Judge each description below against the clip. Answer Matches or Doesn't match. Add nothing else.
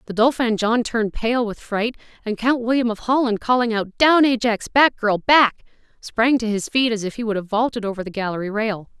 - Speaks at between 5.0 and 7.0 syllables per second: Matches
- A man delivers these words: Doesn't match